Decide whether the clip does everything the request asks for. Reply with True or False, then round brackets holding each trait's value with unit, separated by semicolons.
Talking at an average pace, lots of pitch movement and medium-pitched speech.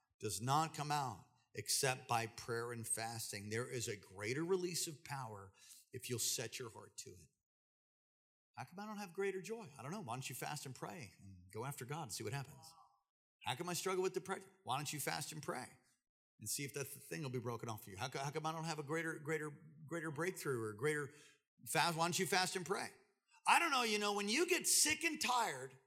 False (240 wpm; 6.6 semitones; 150 Hz)